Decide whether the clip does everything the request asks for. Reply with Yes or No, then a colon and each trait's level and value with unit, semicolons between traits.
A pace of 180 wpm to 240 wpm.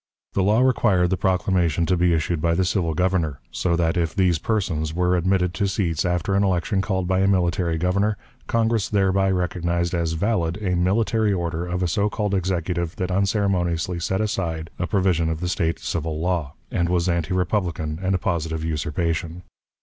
Yes: average, 185 wpm